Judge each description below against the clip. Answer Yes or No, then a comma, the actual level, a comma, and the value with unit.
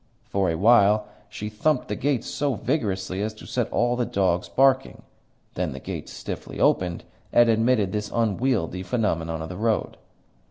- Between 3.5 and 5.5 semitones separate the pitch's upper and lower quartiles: Yes, average, 4.3 semitones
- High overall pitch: No, low, 110 Hz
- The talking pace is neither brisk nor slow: Yes, average, 165 wpm